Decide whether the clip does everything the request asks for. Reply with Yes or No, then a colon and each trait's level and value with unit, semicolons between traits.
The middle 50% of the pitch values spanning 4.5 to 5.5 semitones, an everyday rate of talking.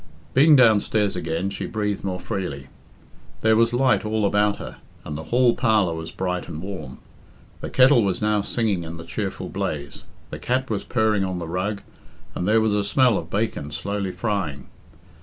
No: average, 4.0 semitones; average, 180 wpm